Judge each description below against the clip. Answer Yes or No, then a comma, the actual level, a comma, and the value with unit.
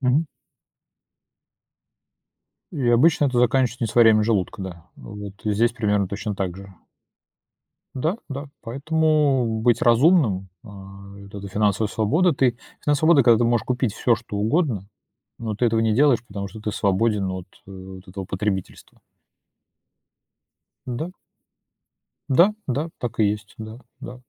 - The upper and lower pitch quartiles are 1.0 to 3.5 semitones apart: No, average, 4.2 semitones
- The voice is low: Yes, low, 115 Hz